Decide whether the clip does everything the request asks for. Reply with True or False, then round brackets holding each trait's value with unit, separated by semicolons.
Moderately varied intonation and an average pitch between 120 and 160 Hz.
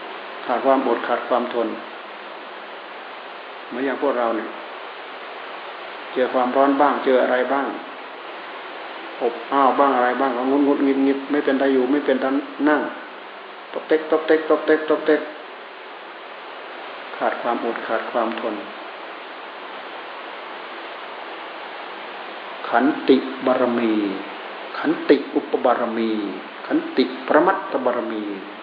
True (3.0 semitones; 135 Hz)